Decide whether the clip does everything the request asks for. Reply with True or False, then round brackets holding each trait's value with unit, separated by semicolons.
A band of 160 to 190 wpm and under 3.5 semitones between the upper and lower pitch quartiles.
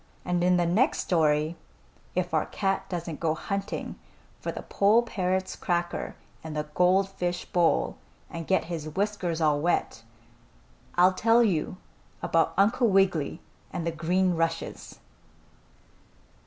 False (135 wpm; 2.8 semitones)